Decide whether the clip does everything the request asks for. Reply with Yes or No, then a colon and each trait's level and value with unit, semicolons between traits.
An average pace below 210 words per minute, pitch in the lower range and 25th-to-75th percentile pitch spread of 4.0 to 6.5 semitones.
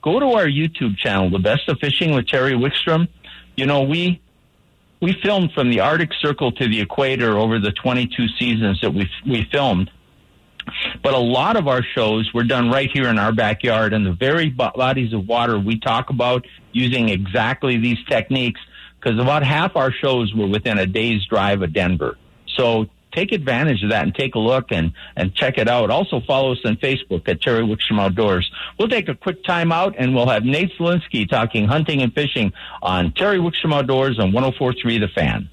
Yes: average, 200 wpm; low, 125 Hz; average, 4.3 semitones